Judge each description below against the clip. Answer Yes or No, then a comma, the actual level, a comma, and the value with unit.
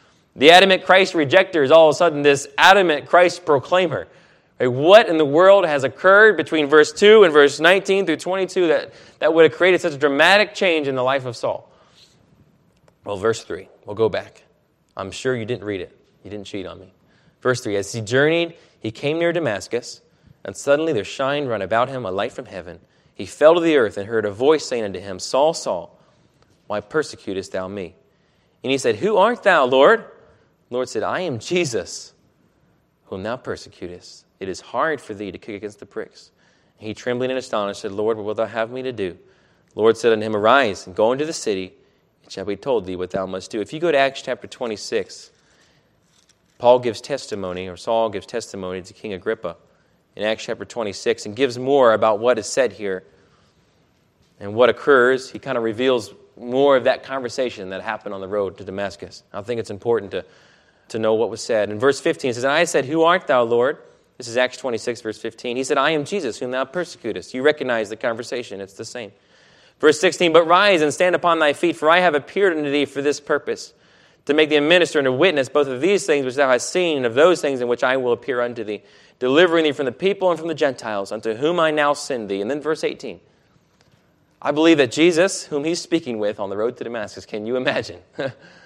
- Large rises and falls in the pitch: Yes, wide, 7.1 semitones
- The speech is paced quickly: Yes, fast, 220 wpm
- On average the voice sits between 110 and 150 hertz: Yes, medium, 140 Hz